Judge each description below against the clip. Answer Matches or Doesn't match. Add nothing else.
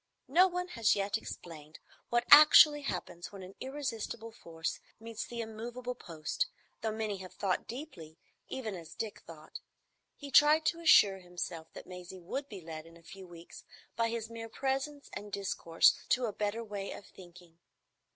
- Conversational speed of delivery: Matches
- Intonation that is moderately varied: Doesn't match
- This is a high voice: Matches